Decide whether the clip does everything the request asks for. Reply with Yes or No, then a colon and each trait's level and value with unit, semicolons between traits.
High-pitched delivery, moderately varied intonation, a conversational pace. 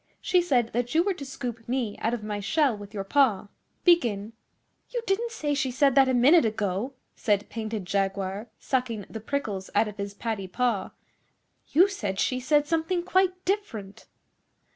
No: high, 240 Hz; wide, 6.3 semitones; average, 175 wpm